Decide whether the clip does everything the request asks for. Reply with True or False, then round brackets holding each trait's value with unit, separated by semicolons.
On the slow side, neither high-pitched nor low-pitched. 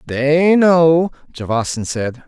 True (105 wpm; 145 Hz)